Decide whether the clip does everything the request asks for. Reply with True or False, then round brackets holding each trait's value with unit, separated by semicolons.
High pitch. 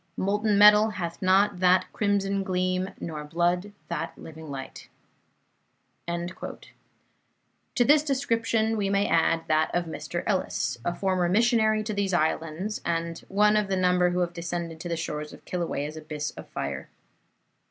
False (180 Hz)